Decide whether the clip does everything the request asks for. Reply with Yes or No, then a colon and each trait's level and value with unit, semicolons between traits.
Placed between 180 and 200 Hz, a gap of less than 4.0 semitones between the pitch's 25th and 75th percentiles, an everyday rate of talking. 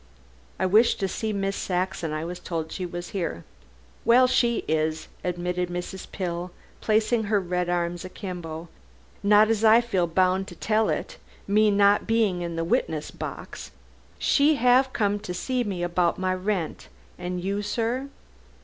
Yes: medium, 185 Hz; average, 3.5 semitones; average, 160 wpm